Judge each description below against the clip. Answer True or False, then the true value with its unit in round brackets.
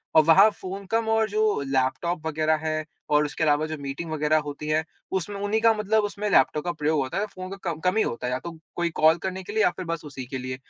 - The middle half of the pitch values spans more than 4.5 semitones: True (4.9 semitones)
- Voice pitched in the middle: True (160 Hz)